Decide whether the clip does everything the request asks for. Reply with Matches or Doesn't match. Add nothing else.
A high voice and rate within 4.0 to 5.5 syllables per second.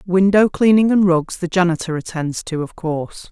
Doesn't match